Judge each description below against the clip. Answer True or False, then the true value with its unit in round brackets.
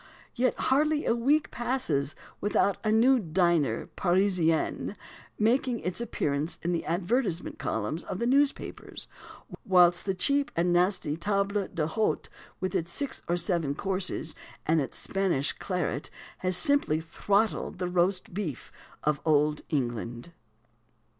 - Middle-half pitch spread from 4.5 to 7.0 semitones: True (5.2 semitones)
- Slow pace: True (130 wpm)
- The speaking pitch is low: False (180 Hz)